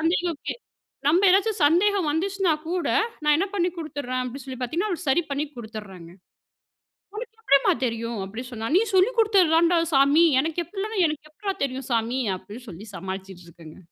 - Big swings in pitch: Yes, wide, 7.4 semitones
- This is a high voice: Yes, very high, 300 Hz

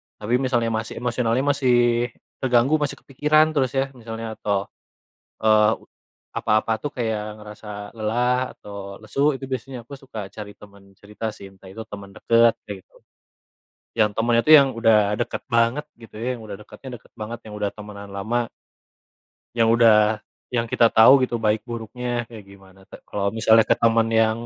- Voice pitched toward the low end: Yes, low, 115 Hz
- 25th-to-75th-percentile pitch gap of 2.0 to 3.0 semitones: Yes, narrow, 2.5 semitones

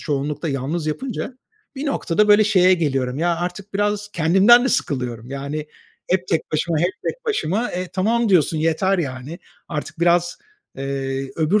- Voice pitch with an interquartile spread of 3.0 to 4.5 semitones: No, wide, 5.5 semitones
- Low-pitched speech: No, medium, 170 Hz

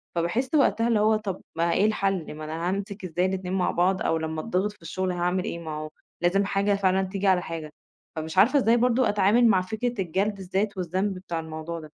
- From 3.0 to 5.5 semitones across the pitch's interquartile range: Yes, average, 3.3 semitones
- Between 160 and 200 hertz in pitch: Yes, high, 190 Hz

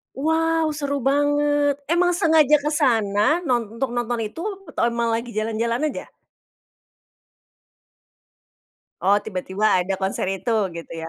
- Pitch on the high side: Yes, high, 245 Hz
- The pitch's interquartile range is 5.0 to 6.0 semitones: Yes, wide, 5.4 semitones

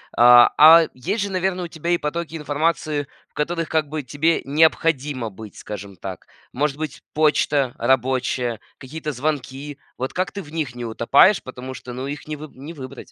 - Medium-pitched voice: Yes, medium, 145 Hz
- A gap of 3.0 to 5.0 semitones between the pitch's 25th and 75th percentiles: Yes, average, 3.9 semitones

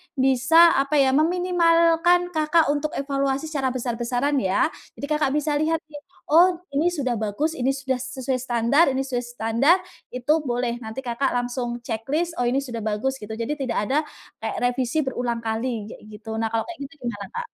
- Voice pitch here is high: Yes, very high, 265 Hz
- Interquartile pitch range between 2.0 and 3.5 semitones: No, average, 4.2 semitones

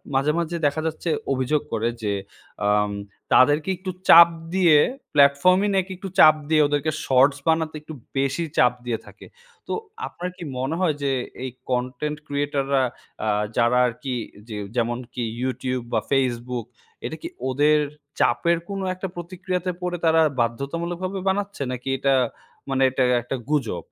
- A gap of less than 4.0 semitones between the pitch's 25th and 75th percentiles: No, average, 5.0 semitones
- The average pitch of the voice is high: No, medium, 140 Hz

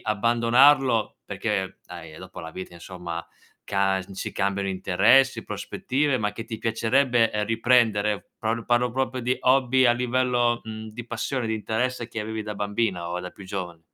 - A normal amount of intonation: Yes, average, 3.8 semitones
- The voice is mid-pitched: No, low, 110 Hz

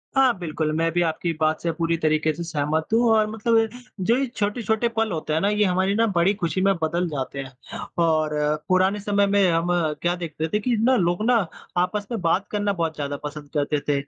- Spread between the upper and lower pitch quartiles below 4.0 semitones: No, average, 4.8 semitones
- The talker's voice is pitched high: No, medium, 175 Hz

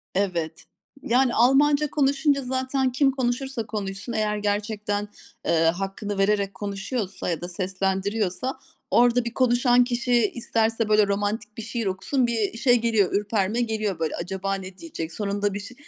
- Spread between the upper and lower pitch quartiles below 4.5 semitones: Yes, average, 3.8 semitones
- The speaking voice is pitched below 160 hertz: No, high, 215 Hz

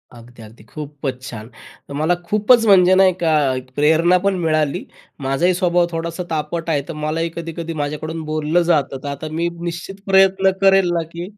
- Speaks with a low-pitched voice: No, medium, 165 Hz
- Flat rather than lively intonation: No, average, 3.0 semitones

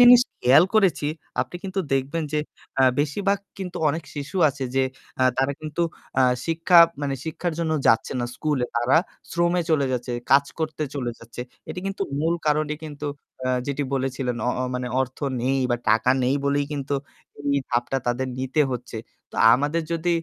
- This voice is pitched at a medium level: Yes, medium, 145 Hz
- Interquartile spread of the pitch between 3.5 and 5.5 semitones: Yes, average, 3.9 semitones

